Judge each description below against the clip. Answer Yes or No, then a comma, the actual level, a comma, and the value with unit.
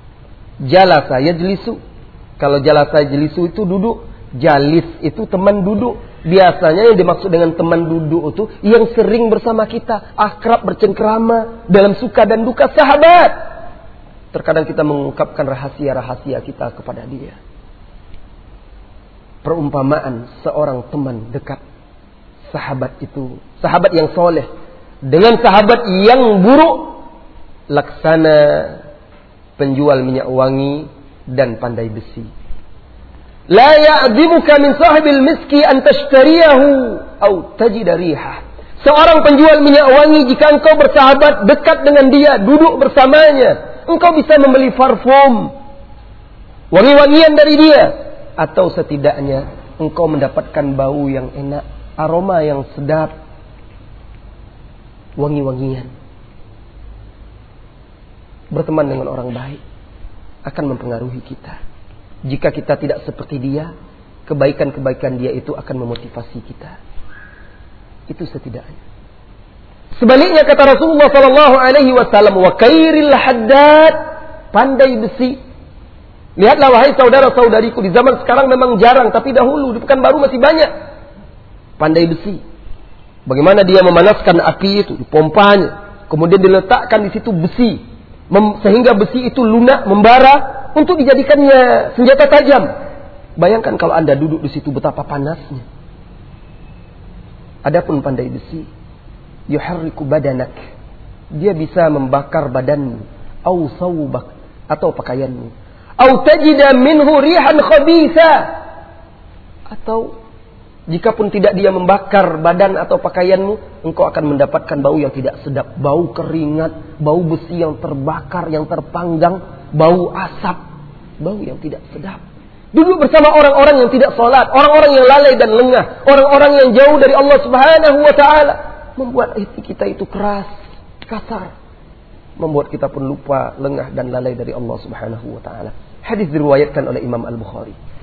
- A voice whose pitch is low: No, medium, 175 Hz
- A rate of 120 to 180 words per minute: No, average, 110 wpm